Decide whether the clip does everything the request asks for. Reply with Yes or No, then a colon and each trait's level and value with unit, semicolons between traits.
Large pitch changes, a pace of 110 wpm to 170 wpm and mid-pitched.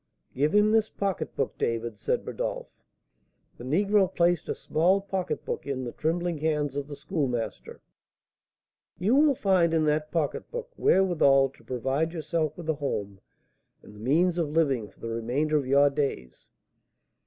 No: average, 4.6 semitones; average, 155 wpm; medium, 155 Hz